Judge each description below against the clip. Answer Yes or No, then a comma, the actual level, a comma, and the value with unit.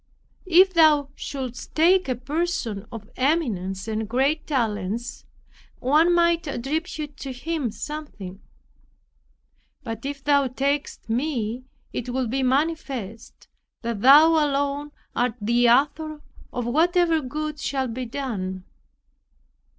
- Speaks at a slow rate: Yes, slow, 115 wpm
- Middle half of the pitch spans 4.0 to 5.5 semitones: Yes, average, 4.6 semitones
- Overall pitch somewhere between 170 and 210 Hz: No, very high, 270 Hz